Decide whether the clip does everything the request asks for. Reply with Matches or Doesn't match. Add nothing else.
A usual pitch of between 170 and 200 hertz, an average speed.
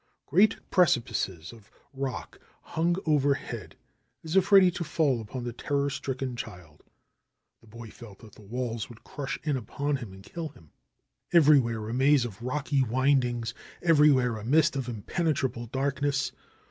Doesn't match